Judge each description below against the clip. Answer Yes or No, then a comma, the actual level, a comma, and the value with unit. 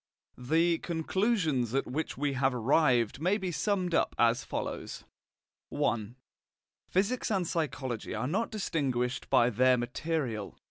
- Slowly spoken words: Yes, slow, 130 wpm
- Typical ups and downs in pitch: No, wide, 6.1 semitones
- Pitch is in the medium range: Yes, medium, 145 Hz